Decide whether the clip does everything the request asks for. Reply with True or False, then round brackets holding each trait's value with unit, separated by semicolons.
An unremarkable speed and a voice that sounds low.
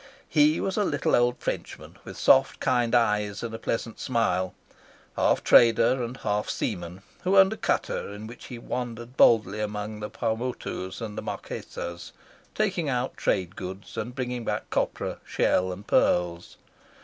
True (160 wpm; 115 Hz)